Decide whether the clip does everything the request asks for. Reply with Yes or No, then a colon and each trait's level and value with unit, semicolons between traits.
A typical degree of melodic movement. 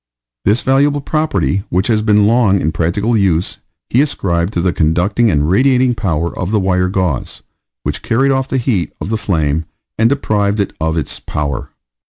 No: wide, 5.7 semitones